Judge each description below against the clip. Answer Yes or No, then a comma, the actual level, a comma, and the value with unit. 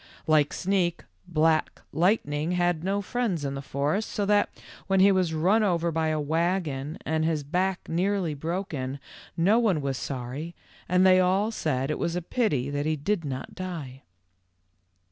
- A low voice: No, medium, 165 Hz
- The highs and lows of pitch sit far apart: No, average, 4.3 semitones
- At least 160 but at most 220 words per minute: Yes, average, 175 wpm